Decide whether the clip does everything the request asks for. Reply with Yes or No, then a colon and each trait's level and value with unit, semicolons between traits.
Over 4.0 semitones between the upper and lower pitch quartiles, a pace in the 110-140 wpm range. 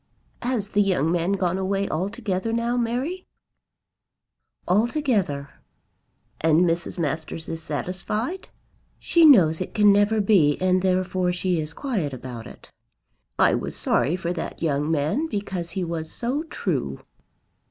Yes: average, 5.2 semitones; slow, 135 wpm